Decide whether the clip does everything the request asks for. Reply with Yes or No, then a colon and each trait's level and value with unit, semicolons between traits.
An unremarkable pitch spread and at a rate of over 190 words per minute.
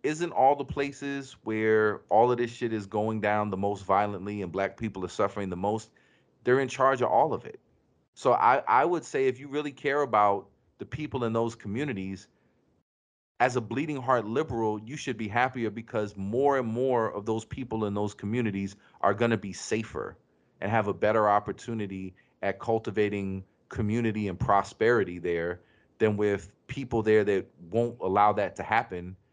No: average, 3.6 semitones; average, 180 wpm